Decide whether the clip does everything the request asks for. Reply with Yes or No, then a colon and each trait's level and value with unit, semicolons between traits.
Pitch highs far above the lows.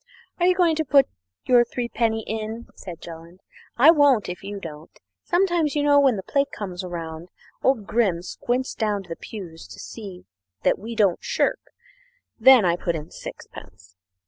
Yes: wide, 7.1 semitones